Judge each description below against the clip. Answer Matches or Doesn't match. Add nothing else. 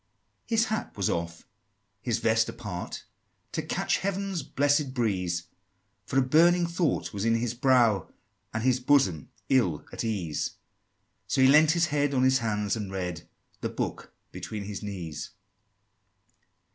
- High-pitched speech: Doesn't match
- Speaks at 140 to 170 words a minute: Matches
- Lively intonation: Matches